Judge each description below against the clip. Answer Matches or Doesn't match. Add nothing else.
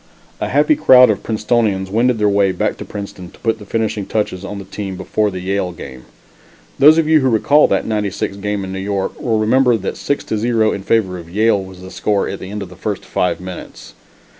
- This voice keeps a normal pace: Doesn't match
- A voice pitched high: Doesn't match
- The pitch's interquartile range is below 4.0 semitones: Matches